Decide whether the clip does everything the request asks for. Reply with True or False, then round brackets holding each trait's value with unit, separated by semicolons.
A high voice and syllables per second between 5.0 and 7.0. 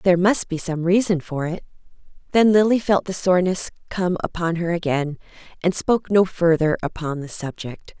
False (175 Hz; 5.1 syllables/s)